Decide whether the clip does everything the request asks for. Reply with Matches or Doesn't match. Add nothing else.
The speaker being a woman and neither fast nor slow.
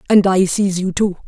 Doesn't match